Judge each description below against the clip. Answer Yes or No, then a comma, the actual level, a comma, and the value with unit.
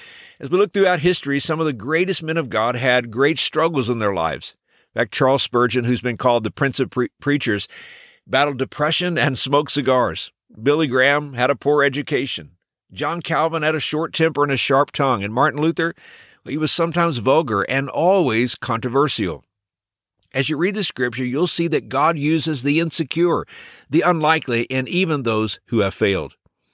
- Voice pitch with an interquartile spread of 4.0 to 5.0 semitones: Yes, average, 4.4 semitones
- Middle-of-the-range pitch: Yes, medium, 145 Hz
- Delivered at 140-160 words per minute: No, average, 185 wpm